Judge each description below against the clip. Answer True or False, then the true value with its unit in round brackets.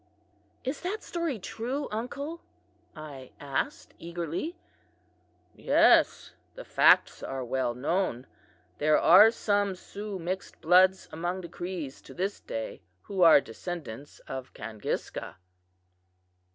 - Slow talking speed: True (110 wpm)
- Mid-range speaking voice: True (180 Hz)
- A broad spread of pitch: True (6.5 semitones)